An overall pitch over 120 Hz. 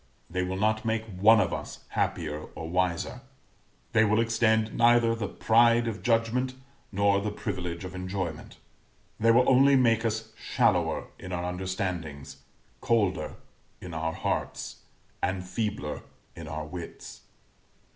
No: low, 100 Hz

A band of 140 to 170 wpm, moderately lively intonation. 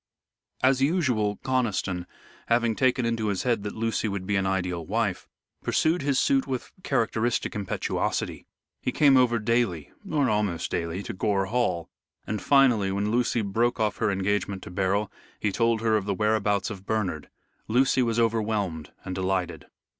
Yes: average, 160 wpm; average, 3.7 semitones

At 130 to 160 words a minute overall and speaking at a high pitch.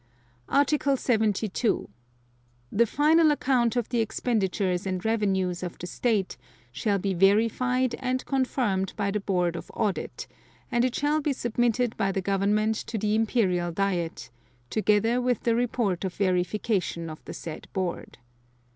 Yes: average, 145 wpm; high, 215 Hz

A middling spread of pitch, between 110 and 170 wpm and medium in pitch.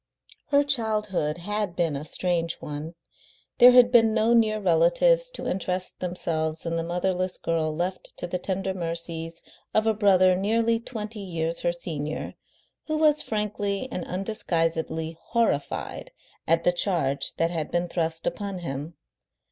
Yes: average, 4.4 semitones; average, 150 wpm; medium, 180 Hz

